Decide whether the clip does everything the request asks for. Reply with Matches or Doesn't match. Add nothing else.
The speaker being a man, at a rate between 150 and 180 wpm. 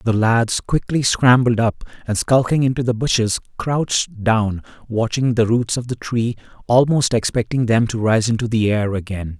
Matches